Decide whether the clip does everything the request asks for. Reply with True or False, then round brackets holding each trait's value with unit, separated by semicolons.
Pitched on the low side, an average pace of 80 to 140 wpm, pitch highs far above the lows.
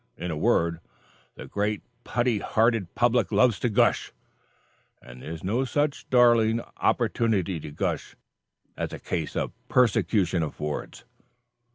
True (105 Hz; 135 wpm; 6.2 semitones)